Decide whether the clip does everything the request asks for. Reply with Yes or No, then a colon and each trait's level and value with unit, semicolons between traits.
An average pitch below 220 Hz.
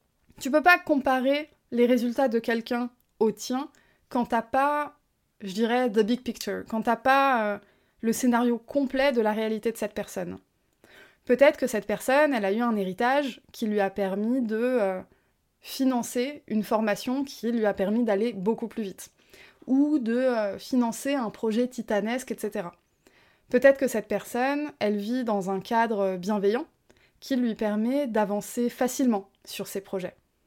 No: high, 235 Hz